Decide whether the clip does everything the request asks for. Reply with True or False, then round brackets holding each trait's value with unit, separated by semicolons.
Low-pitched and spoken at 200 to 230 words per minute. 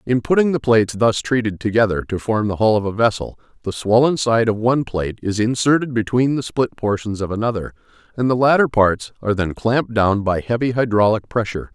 True (115 Hz; 205 wpm)